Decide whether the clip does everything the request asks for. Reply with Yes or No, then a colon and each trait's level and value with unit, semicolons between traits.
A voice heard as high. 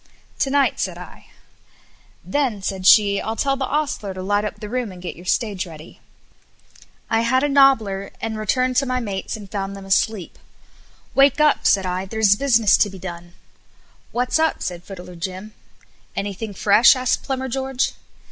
Yes: high, 215 Hz